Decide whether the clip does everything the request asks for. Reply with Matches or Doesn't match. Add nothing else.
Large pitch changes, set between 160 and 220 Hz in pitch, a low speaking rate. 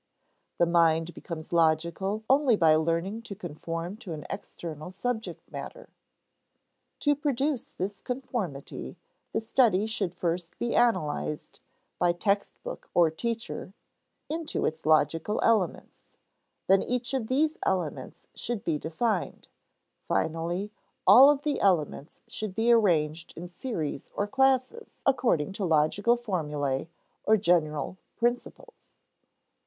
Matches